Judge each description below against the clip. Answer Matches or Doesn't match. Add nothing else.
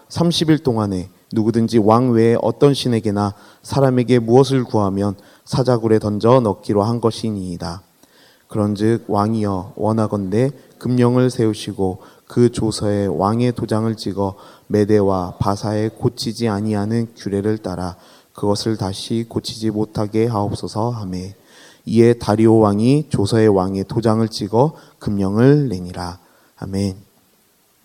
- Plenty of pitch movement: Doesn't match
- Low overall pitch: Matches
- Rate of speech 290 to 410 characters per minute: Doesn't match